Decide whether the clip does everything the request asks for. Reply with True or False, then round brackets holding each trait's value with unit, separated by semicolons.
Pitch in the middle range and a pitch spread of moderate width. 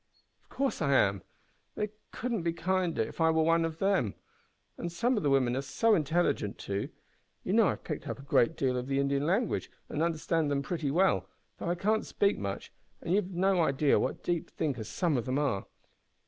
True (160 Hz; 5.0 semitones)